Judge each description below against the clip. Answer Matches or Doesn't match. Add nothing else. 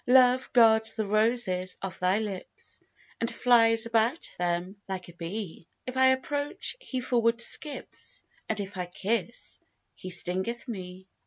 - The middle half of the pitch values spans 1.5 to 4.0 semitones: Doesn't match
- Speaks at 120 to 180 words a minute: Matches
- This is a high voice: Matches